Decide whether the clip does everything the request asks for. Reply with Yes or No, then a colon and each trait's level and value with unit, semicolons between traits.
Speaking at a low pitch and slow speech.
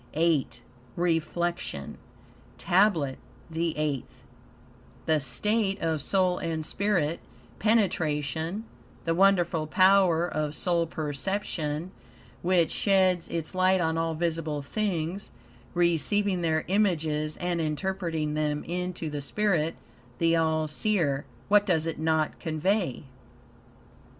No: medium, 165 Hz; slow, 105 wpm